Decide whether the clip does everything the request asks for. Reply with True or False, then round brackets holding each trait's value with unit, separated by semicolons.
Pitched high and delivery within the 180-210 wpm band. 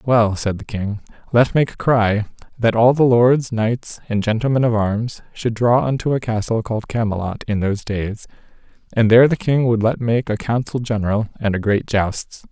False (115 Hz; 195 wpm)